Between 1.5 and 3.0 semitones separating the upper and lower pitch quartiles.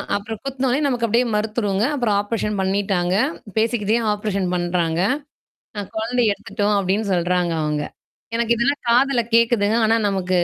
No: average, 3.5 semitones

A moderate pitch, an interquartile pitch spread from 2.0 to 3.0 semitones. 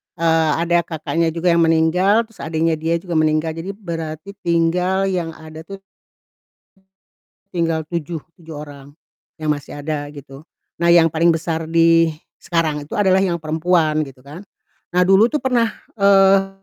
Yes: medium, 165 Hz; narrow, 2.4 semitones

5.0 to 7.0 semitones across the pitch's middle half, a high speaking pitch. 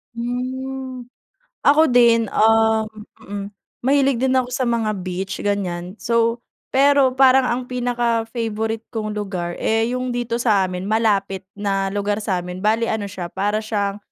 No: average, 3.4 semitones; high, 225 Hz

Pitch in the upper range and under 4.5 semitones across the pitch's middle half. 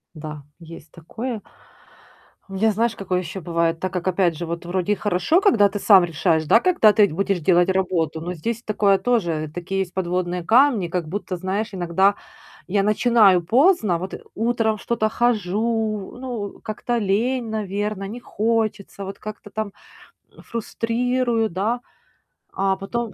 Yes: high, 200 Hz; average, 4.0 semitones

